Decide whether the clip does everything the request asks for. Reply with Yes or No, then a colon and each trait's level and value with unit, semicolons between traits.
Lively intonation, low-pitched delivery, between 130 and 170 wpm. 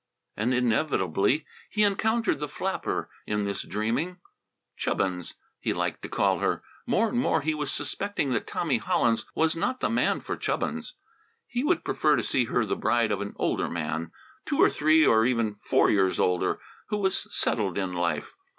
No: wide, 8.1 semitones; low, 120 Hz; average, 180 wpm